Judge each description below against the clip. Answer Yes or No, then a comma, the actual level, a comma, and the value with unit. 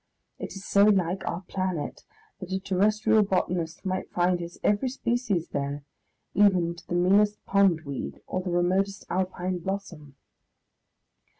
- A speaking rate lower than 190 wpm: Yes, slow, 135 wpm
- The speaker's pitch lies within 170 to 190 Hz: Yes, medium, 185 Hz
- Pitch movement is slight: Yes, narrow, 2.3 semitones